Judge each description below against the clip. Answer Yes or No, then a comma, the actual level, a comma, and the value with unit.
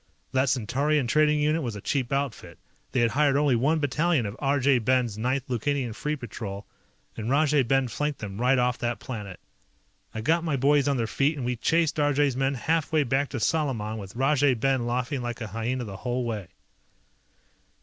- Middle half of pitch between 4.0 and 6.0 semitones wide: No, average, 3.6 semitones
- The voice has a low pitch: Yes, low, 130 Hz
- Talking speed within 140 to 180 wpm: No, average, 190 wpm